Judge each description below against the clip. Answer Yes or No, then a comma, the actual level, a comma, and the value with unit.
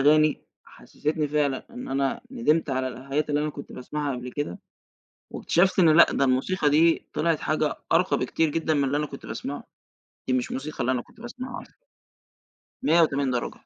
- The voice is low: No, medium, 150 Hz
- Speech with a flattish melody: No, average, 3.0 semitones